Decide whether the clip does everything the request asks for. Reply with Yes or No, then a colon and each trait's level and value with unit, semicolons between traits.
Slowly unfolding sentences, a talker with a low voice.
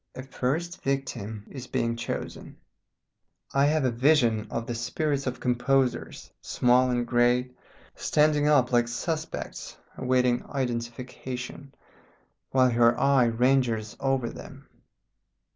Yes: slow, 115 wpm; low, 125 Hz